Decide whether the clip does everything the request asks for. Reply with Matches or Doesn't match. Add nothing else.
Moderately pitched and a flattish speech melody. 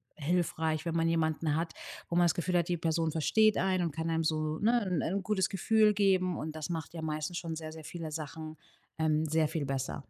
Matches